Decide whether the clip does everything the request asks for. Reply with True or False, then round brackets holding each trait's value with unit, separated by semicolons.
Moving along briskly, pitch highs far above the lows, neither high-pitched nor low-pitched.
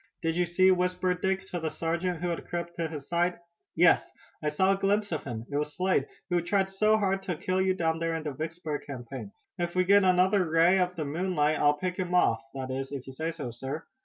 False (240 wpm; 3.5 semitones; 170 Hz)